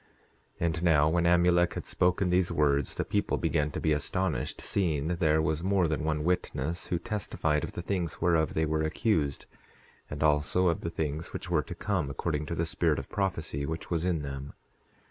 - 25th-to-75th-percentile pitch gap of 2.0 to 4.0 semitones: Yes, narrow, 2.6 semitones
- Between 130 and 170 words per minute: No, average, 200 wpm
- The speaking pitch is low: Yes, very low, 80 Hz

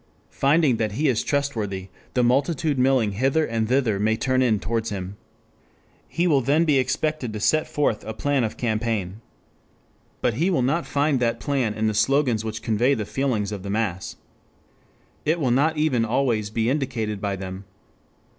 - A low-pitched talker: Yes, low, 120 Hz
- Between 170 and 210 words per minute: Yes, average, 175 wpm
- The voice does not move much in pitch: No, average, 4.5 semitones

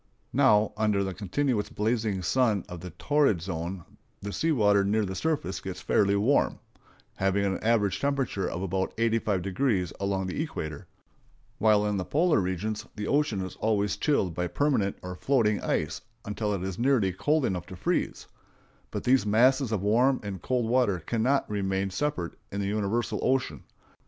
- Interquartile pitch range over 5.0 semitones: No, average, 4.4 semitones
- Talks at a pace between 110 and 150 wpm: No, average, 160 wpm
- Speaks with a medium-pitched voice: No, low, 105 Hz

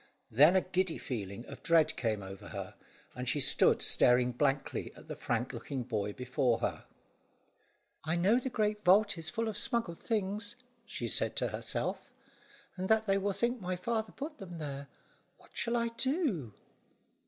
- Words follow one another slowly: No, average, 170 wpm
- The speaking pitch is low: No, medium, 180 Hz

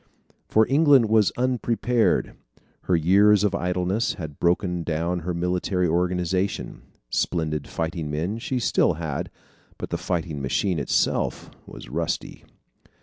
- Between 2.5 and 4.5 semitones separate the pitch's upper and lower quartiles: Yes, average, 4.2 semitones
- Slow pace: Yes, slow, 125 wpm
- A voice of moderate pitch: No, very low, 90 Hz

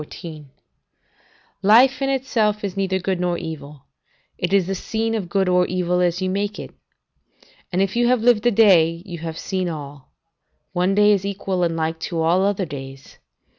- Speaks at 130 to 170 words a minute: No, average, 185 wpm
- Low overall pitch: No, medium, 185 Hz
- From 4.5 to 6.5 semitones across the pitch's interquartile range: No, average, 3.3 semitones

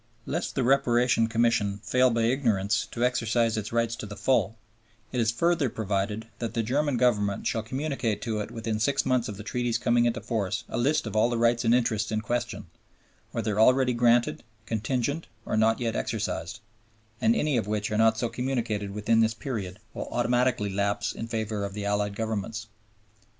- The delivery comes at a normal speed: Yes, average, 185 wpm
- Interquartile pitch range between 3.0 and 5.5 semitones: No, narrow, 2.4 semitones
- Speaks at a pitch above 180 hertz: No, low, 115 Hz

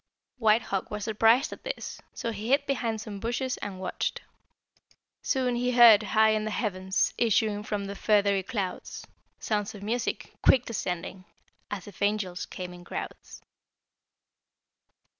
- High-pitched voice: Yes, high, 210 Hz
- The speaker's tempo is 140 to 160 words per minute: Yes, average, 145 wpm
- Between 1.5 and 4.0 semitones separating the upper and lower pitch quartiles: Yes, average, 2.7 semitones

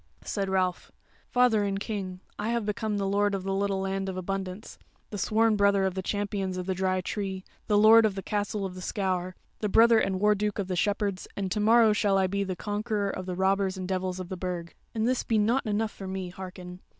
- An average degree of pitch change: No, narrow, 1.9 semitones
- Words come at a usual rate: No, fast, 235 wpm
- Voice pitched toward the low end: No, high, 195 Hz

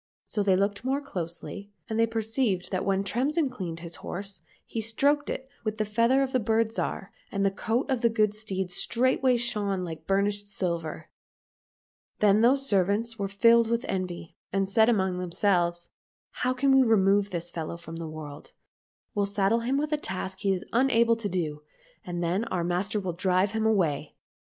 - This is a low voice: No, high, 205 Hz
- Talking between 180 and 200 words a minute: Yes, average, 185 wpm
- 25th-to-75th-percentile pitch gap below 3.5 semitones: No, average, 4.0 semitones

